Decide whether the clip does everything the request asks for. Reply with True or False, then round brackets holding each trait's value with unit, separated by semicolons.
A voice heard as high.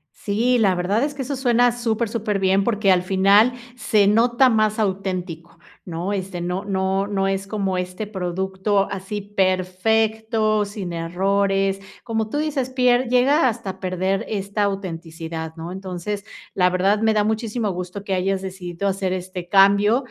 True (195 Hz)